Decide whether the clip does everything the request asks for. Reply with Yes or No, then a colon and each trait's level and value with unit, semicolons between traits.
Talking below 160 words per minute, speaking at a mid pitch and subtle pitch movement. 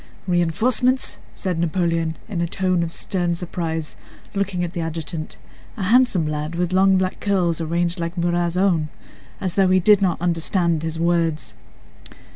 Yes: average, 145 wpm; medium, 175 Hz; narrow, 2.2 semitones